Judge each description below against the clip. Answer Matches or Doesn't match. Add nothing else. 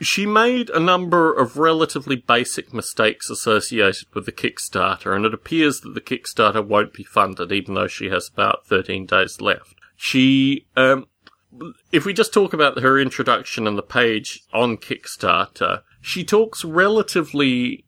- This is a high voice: Doesn't match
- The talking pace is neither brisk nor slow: Matches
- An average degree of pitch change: Doesn't match